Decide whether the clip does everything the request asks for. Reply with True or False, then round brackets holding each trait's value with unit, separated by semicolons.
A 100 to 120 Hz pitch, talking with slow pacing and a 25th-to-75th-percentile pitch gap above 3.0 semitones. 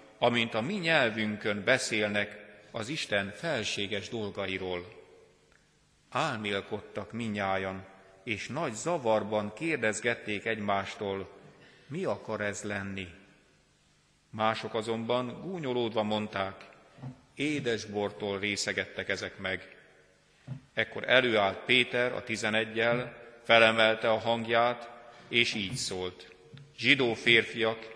False (110 Hz; 90 wpm; 2.7 semitones)